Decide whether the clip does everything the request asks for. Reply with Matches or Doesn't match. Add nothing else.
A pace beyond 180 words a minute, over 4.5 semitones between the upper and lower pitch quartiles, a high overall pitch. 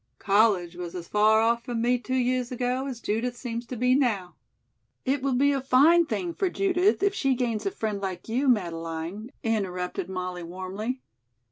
Matches